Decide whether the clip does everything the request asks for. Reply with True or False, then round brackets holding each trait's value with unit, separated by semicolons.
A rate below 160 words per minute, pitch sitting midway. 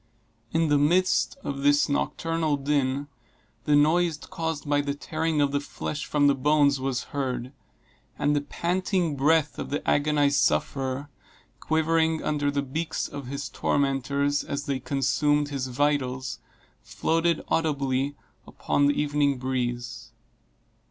True (135 wpm; 145 Hz)